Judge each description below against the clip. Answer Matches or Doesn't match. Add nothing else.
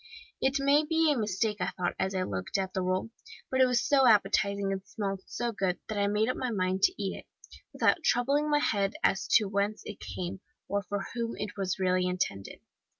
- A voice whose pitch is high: Matches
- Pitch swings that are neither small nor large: Matches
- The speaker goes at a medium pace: Doesn't match